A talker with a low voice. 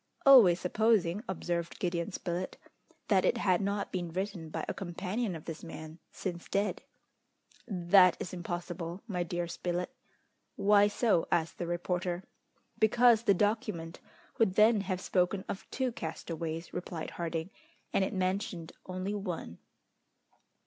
No: medium, 180 Hz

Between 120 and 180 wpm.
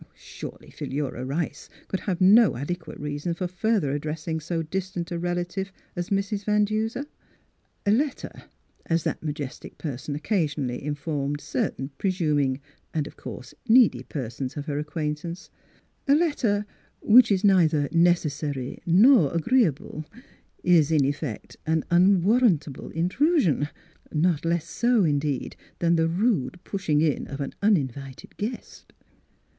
Yes: average, 140 wpm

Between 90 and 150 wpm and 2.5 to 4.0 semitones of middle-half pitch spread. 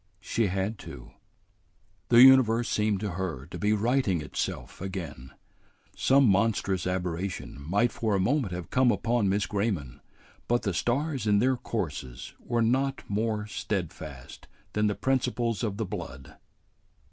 No: average, 145 wpm; average, 4.4 semitones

